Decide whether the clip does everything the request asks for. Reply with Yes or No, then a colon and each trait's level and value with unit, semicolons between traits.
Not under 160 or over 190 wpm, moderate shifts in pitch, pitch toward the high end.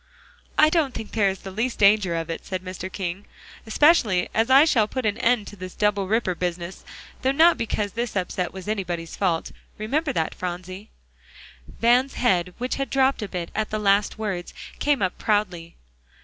Yes: average, 185 wpm; average, 4.6 semitones; high, 205 Hz